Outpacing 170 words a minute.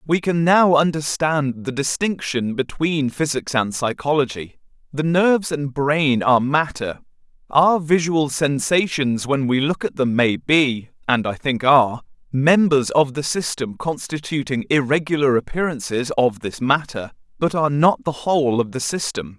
No: average, 150 wpm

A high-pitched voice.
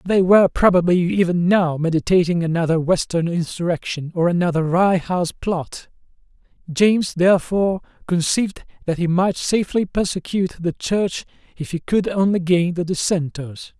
No: medium, 175 Hz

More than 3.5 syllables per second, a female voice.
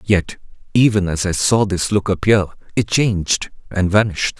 No: 4.9 syllables/s; male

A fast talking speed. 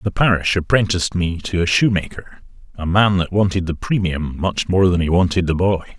Yes: fast, 210 wpm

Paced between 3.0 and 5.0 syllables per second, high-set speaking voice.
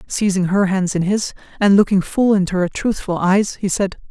Yes: 4.9 syllables/s; high, 195 Hz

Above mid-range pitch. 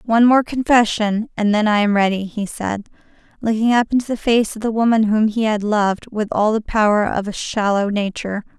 Yes: high, 215 Hz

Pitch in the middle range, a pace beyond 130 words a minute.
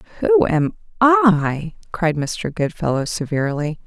No: medium, 180 Hz; slow, 110 wpm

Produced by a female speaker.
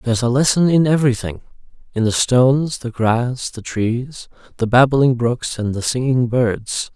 No: male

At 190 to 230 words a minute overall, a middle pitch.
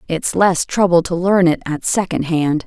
Yes: average, 200 wpm; medium, 175 Hz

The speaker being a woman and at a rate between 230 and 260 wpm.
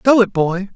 No: male; fast, 240 wpm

